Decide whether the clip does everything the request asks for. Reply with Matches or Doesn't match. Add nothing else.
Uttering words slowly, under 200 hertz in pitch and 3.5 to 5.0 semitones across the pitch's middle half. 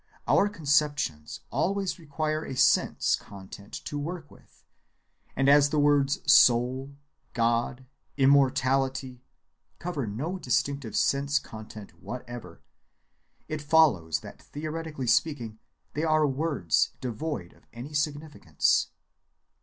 Matches